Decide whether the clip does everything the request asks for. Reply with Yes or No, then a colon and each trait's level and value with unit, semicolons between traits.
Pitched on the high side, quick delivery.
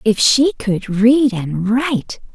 No: high, 230 Hz; average, 155 wpm